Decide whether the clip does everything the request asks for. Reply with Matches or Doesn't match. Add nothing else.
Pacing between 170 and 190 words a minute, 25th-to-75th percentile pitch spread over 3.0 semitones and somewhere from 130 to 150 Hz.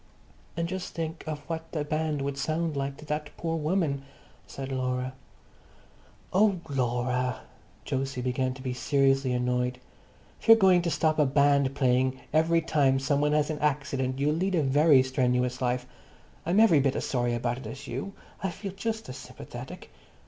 Matches